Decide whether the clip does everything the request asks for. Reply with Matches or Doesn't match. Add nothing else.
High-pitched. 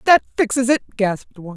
Matches